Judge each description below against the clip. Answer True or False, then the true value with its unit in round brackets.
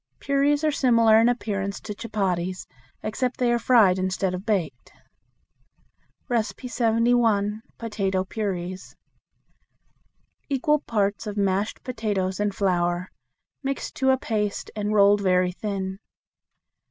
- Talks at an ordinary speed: False (115 wpm)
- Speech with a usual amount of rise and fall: True (3.6 semitones)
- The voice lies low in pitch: False (210 Hz)